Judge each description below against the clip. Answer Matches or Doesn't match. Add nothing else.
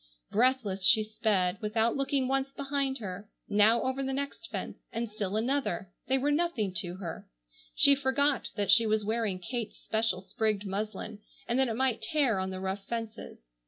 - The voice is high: Matches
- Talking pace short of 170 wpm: Doesn't match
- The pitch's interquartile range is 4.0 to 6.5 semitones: Matches